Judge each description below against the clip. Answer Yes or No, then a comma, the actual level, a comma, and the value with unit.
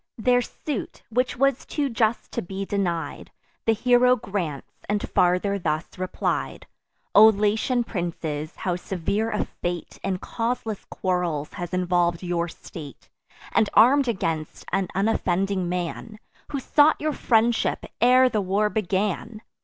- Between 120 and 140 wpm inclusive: Yes, slow, 135 wpm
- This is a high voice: Yes, high, 200 Hz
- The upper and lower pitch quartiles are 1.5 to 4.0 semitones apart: No, average, 4.6 semitones